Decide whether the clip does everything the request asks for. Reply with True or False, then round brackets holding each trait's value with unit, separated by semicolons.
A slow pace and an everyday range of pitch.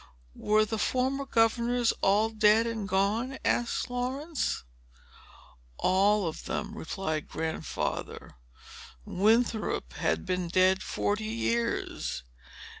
True (100 wpm; 3.8 semitones)